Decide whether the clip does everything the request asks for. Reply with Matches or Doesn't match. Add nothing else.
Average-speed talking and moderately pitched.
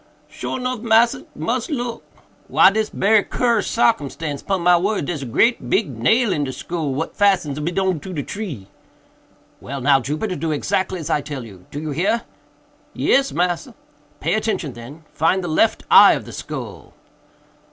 Matches